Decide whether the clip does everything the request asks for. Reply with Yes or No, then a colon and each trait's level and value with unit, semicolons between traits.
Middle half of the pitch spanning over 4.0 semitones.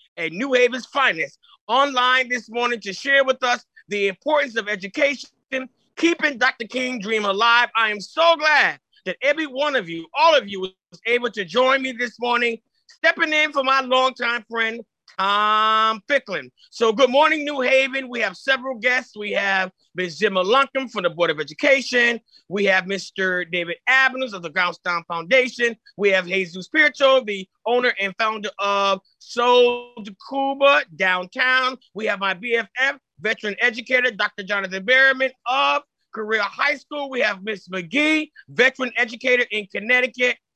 Yes: average, 4.8 semitones